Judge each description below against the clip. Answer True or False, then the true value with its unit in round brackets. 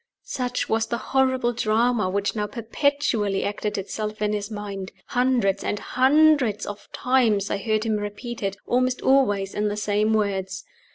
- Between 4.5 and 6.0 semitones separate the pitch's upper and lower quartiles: False (3.3 semitones)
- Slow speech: False (160 wpm)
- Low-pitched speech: False (215 Hz)